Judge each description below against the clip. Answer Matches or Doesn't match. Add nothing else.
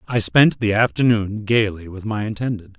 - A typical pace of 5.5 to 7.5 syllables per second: Doesn't match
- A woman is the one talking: Doesn't match